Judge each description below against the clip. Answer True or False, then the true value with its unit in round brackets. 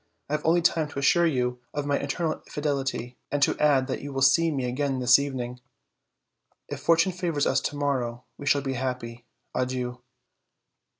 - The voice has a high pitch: False (140 Hz)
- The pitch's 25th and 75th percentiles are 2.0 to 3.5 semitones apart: True (2.8 semitones)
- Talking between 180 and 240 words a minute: True (185 wpm)